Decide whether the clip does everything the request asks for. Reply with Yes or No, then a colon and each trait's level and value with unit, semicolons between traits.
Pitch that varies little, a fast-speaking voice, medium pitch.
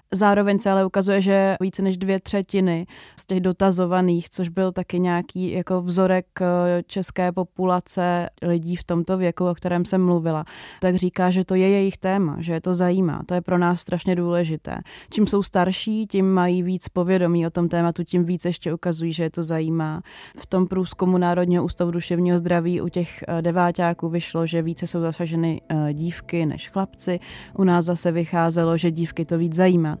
Yes: narrow, 1.5 semitones; fast, 180 wpm; medium, 180 Hz